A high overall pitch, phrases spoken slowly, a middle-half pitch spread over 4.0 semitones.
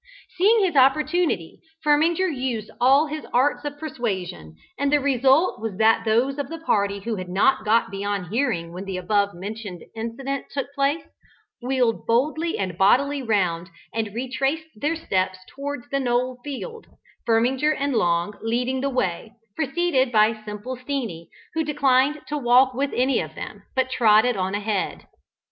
No: very high, 250 Hz; average, 160 wpm; average, 5.1 semitones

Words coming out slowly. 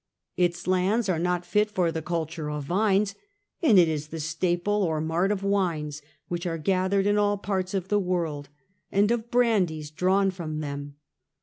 No: average, 180 wpm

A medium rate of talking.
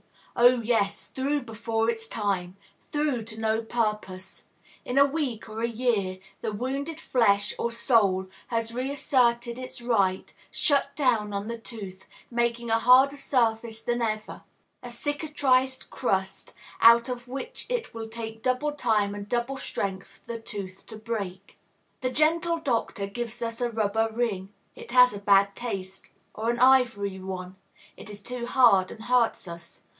Yes: average, 160 wpm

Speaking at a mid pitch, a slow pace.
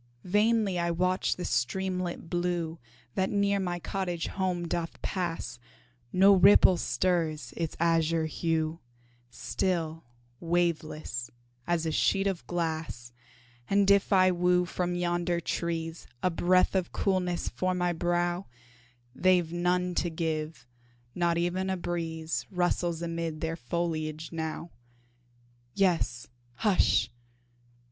Yes: medium, 175 Hz; slow, 120 wpm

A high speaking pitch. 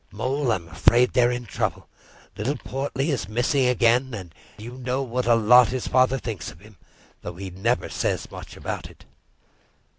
No: low, 120 Hz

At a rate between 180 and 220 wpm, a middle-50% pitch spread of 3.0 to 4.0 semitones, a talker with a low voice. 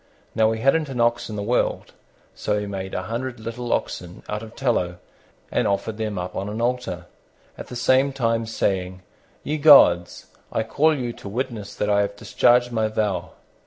Yes: average, 190 wpm; average, 3.3 semitones; low, 110 Hz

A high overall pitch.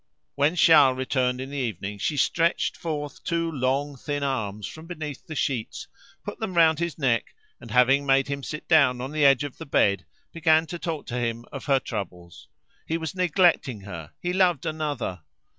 No: medium, 140 Hz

